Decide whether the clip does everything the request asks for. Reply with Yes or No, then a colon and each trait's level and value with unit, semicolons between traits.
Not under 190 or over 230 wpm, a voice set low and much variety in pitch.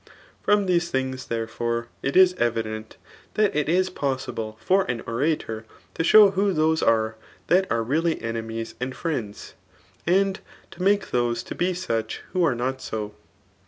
No: average, 145 wpm; low, 130 Hz; wide, 7.9 semitones